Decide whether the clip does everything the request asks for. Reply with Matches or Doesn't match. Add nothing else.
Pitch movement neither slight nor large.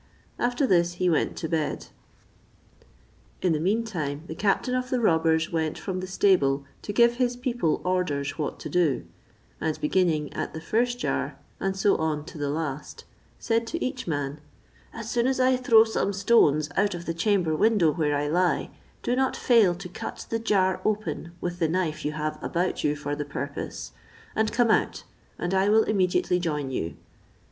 Doesn't match